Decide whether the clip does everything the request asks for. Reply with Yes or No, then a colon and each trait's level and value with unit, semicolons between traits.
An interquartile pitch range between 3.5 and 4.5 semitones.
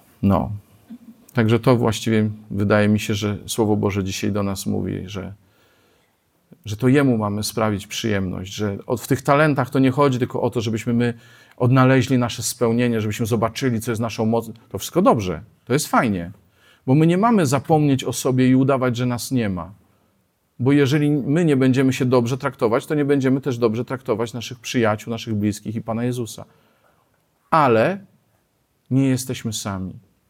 Yes: average, 3.8 semitones